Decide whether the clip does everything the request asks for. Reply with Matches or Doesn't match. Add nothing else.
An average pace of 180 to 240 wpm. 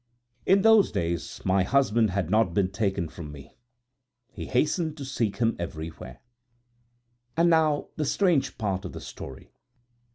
Doesn't match